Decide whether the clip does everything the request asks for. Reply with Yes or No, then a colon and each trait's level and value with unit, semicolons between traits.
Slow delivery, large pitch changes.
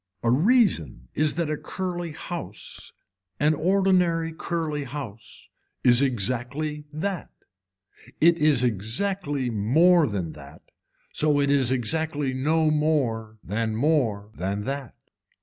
Yes: slow, 115 wpm; wide, 5.7 semitones